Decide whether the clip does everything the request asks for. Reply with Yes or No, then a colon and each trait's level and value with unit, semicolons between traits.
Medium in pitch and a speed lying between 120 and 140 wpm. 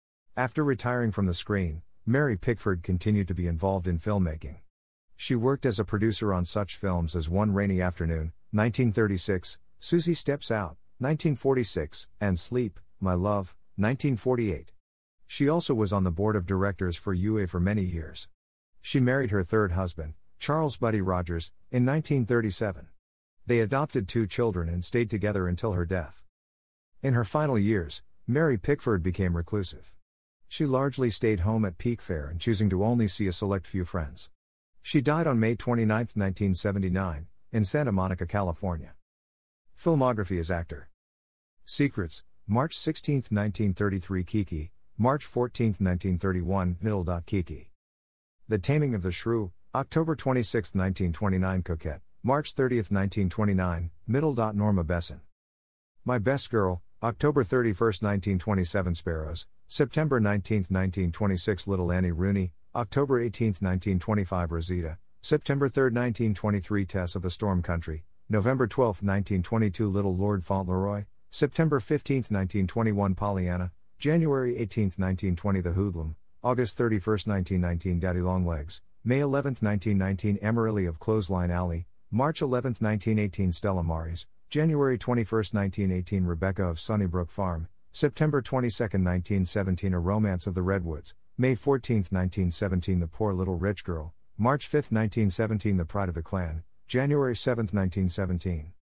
No: low, 100 Hz; slow, 135 wpm